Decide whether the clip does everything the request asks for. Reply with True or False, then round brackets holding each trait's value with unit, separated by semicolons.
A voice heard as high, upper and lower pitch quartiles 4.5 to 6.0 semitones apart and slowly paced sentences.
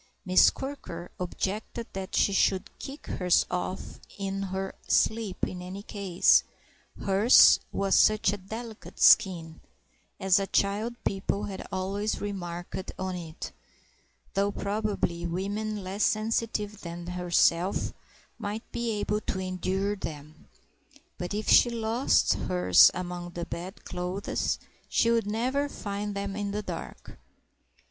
False (195 Hz; 2.7 semitones; 125 wpm)